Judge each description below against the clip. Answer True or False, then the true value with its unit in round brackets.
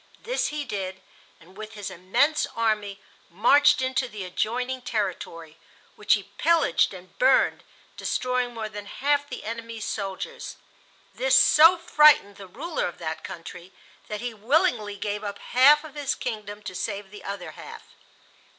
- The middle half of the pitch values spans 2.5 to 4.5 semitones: False (5.6 semitones)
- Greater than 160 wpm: False (150 wpm)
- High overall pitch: True (220 Hz)